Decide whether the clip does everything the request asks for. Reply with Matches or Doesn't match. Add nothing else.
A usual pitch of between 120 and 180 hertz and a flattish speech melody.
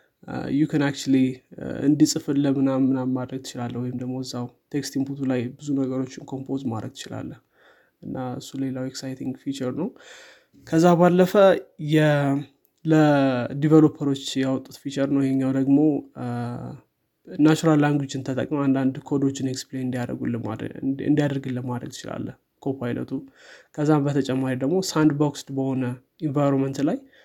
Matches